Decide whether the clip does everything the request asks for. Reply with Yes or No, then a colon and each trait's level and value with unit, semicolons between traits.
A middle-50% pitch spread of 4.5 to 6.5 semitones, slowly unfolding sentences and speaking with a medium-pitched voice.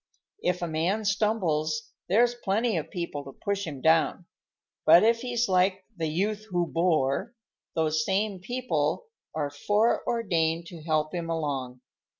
No: average, 5.1 semitones; average, 145 wpm; medium, 175 Hz